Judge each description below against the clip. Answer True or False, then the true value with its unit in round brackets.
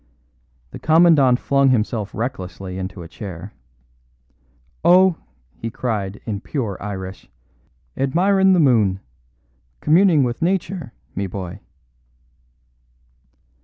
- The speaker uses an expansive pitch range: True (8.7 semitones)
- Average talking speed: False (95 wpm)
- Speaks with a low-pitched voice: True (120 Hz)